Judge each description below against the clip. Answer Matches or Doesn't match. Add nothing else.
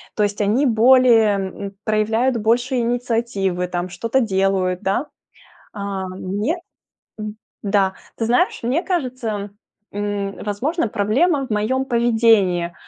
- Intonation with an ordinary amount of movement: Matches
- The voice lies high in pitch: Matches